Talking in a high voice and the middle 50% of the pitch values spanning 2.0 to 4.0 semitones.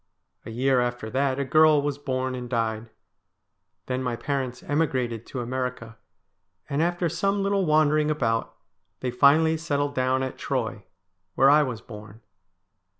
No: low, 130 Hz; average, 3.7 semitones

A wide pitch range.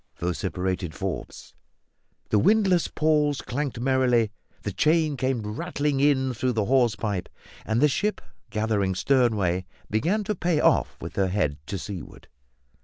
Yes: wide, 6.4 semitones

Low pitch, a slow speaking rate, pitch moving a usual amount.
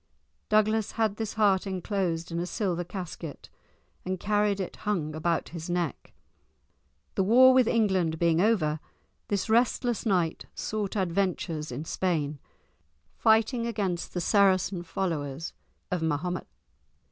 No: medium, 185 Hz; slow, 125 wpm; average, 4.0 semitones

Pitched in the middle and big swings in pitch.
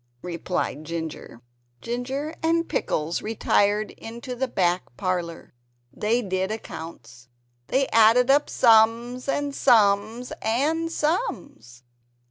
No: high, 225 Hz; wide, 6.5 semitones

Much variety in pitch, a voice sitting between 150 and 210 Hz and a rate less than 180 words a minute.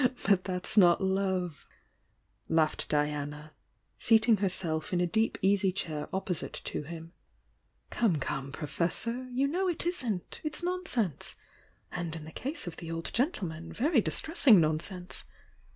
Yes: wide, 6.3 semitones; medium, 185 Hz; average, 150 wpm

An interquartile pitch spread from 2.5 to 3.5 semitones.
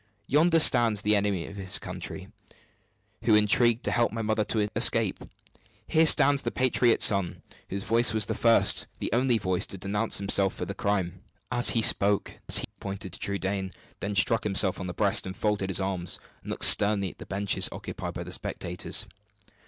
Yes: average, 2.9 semitones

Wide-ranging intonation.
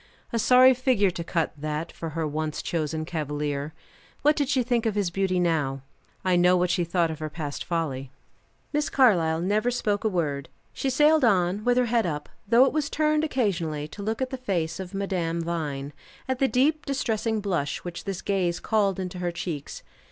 Yes: wide, 6.6 semitones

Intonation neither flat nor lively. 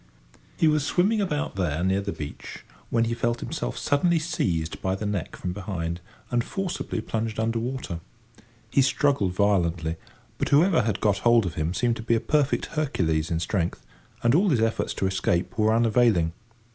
No: wide, 6.6 semitones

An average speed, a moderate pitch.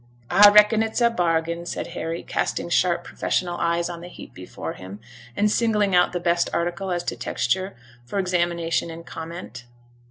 Yes: average, 170 wpm; medium, 175 Hz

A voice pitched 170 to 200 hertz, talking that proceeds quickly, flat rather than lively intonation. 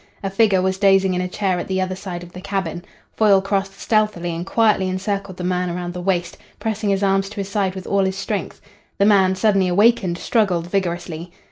Yes: high, 190 Hz; fast, 215 wpm; narrow, 1.8 semitones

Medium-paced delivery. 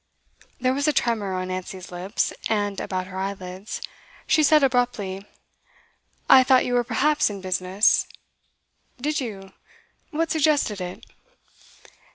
No: slow, 130 wpm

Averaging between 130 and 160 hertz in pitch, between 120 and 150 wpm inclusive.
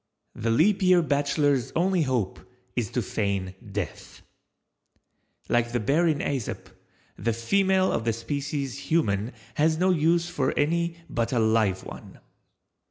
Yes: medium, 140 Hz; average, 140 wpm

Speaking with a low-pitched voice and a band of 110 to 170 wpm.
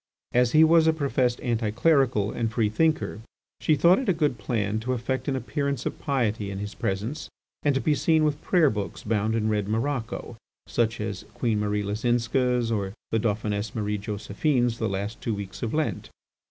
No: low, 115 Hz; average, 190 wpm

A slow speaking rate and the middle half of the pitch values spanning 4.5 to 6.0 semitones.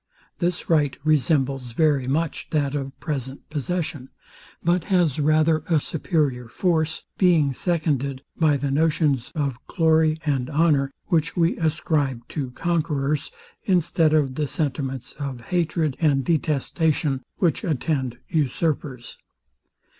No: slow, 120 wpm; average, 3.0 semitones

